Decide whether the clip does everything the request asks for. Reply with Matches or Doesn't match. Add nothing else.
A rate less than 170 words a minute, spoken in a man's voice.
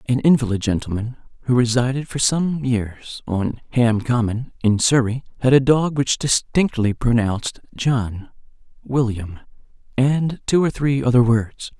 Matches